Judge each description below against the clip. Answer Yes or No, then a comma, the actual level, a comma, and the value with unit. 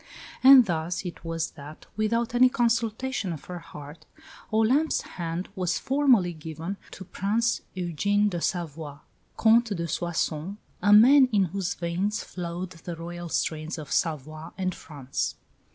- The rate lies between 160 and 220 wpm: No, average, 140 wpm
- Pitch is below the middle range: No, medium, 180 Hz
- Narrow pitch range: No, average, 4.8 semitones